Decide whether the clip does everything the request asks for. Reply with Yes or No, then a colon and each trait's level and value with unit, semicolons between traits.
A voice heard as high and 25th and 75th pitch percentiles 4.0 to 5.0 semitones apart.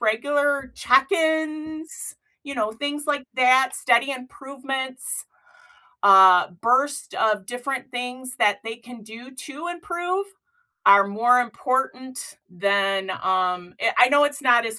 Yes: very high, 255 Hz; average, 4.5 semitones